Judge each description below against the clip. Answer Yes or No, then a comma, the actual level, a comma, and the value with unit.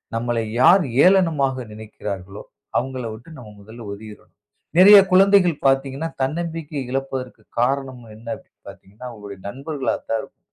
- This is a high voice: No, low, 130 Hz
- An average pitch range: No, wide, 5.7 semitones